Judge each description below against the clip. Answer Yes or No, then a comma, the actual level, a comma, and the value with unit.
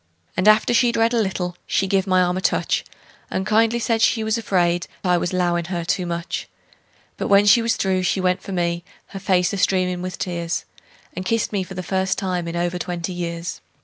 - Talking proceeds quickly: Yes, fast, 215 wpm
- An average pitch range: No, narrow, 2.2 semitones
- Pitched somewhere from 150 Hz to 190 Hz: Yes, medium, 185 Hz